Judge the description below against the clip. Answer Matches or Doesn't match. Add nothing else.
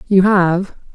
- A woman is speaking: Matches